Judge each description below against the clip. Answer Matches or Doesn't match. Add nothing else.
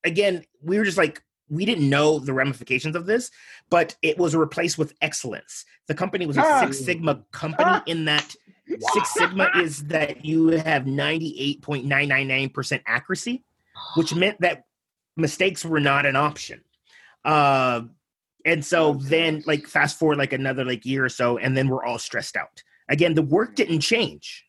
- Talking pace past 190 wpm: Doesn't match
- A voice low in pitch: Doesn't match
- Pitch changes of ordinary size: Matches